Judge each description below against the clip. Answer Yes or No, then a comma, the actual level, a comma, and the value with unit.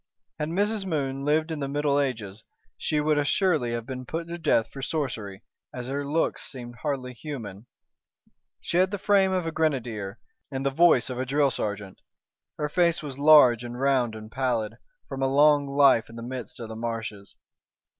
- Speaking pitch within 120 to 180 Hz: Yes, low, 135 Hz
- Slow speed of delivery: No, average, 185 wpm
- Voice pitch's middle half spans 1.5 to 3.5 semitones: No, average, 4.4 semitones